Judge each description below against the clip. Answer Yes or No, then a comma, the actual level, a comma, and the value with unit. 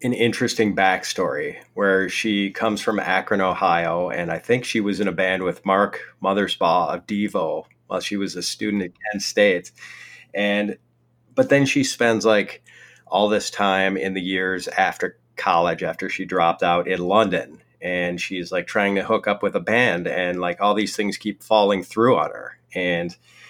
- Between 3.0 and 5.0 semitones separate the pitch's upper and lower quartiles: No, narrow, 2.5 semitones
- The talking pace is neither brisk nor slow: Yes, average, 180 wpm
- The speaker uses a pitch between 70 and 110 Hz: Yes, low, 100 Hz